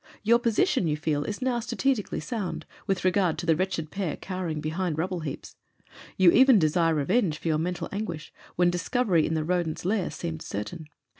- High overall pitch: No, medium, 175 Hz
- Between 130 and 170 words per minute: No, average, 180 wpm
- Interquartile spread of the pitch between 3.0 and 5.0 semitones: Yes, average, 4.3 semitones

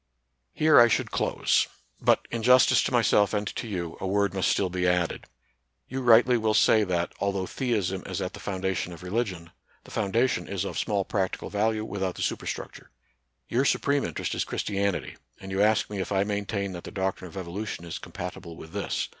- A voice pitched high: No, low, 100 Hz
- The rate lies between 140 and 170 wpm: No, average, 200 wpm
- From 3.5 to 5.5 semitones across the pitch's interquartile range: No, average, 3.0 semitones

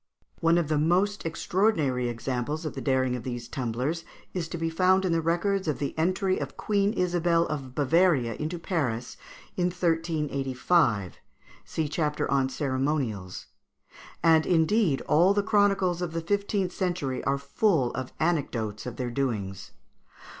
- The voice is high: No, medium, 160 Hz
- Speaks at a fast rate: No, average, 155 wpm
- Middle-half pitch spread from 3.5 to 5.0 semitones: No, wide, 5.4 semitones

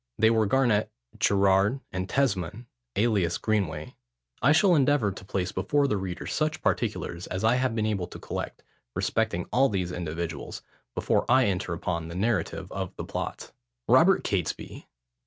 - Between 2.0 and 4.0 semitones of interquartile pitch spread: No, average, 5.1 semitones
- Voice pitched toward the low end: Yes, low, 100 Hz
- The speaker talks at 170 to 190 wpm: No, average, 155 wpm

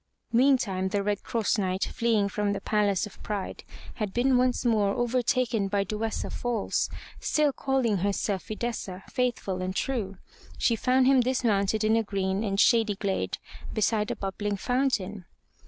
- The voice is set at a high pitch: Yes, high, 215 Hz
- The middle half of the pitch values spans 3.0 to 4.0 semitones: Yes, average, 3.4 semitones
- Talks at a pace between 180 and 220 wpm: No, average, 155 wpm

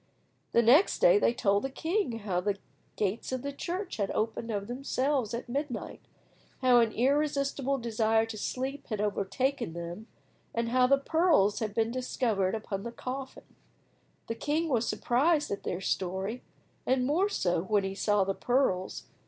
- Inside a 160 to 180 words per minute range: Yes, average, 165 wpm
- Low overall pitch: No, high, 235 Hz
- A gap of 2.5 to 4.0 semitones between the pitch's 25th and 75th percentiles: No, average, 4.9 semitones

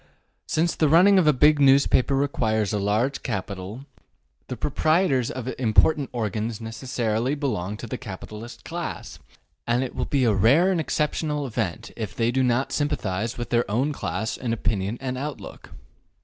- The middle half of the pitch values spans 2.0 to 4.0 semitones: No, average, 4.5 semitones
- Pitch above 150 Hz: No, low, 125 Hz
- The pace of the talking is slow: No, average, 165 wpm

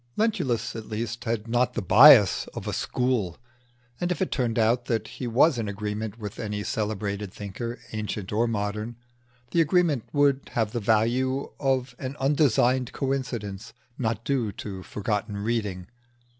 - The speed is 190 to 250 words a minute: No, average, 155 wpm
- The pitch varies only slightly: No, average, 3.7 semitones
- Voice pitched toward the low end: Yes, low, 115 Hz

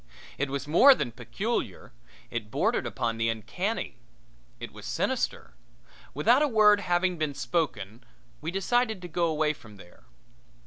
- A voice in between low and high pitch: Yes, medium, 155 Hz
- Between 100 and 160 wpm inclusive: Yes, average, 145 wpm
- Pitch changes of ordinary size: No, wide, 8.6 semitones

